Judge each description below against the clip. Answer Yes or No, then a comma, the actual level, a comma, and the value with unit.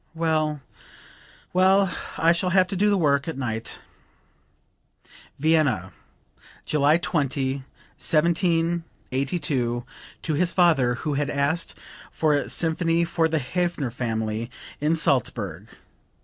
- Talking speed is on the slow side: Yes, slow, 110 wpm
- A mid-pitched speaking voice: Yes, medium, 155 Hz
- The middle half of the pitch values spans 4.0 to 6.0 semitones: Yes, average, 4.3 semitones